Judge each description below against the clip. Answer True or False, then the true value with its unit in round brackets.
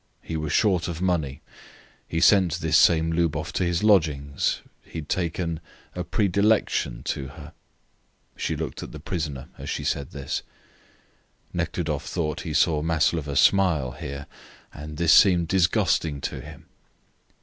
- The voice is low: True (80 Hz)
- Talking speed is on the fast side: False (145 wpm)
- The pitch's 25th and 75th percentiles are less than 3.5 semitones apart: True (2.9 semitones)